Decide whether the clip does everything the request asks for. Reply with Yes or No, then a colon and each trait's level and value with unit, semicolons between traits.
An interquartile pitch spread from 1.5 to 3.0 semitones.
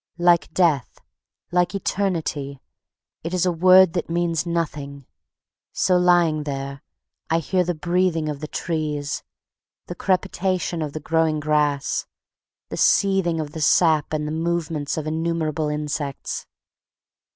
Yes: narrow, 2.6 semitones